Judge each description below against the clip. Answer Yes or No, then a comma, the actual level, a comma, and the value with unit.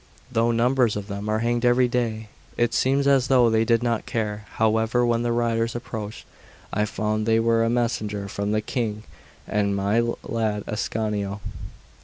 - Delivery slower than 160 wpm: No, average, 170 wpm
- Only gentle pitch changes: Yes, narrow, 2.0 semitones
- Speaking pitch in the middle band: No, low, 115 Hz